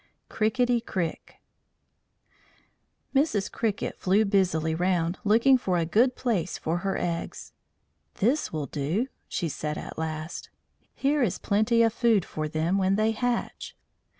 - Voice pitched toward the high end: Yes, high, 195 Hz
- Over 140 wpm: No, slow, 135 wpm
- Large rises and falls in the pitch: Yes, wide, 5.8 semitones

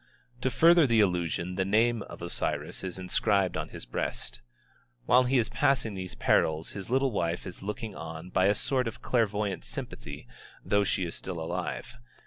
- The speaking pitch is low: Yes, low, 100 Hz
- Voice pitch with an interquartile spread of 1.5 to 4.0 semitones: No, average, 4.5 semitones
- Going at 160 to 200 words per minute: Yes, average, 175 wpm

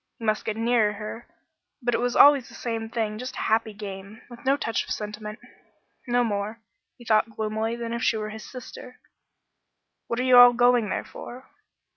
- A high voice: Yes, high, 225 Hz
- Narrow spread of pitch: Yes, narrow, 2.2 semitones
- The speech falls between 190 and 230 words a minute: Yes, average, 195 wpm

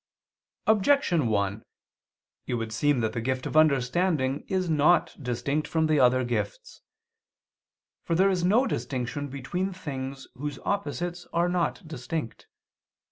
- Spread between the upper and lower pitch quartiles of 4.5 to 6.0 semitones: Yes, wide, 5.5 semitones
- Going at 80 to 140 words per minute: Yes, slow, 135 wpm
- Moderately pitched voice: Yes, medium, 150 Hz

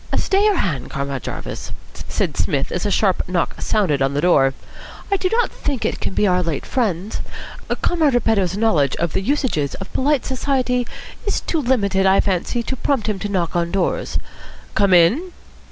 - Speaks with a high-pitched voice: Yes, high, 200 Hz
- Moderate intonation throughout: No, wide, 7.1 semitones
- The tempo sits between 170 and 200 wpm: Yes, average, 180 wpm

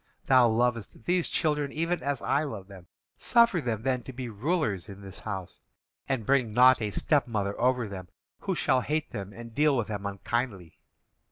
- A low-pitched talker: Yes, low, 120 Hz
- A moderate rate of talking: Yes, average, 180 wpm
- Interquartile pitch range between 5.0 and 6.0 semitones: Yes, average, 5.3 semitones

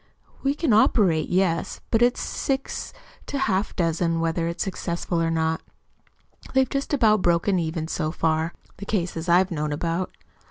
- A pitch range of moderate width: Yes, average, 4.3 semitones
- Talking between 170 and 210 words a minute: No, average, 160 wpm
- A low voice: No, medium, 175 Hz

